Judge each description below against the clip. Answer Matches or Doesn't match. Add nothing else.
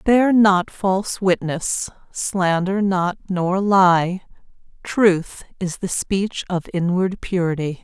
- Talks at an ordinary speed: Doesn't match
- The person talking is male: Doesn't match